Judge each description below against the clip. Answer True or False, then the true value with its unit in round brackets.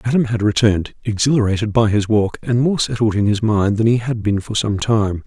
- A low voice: True (110 Hz)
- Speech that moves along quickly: True (230 wpm)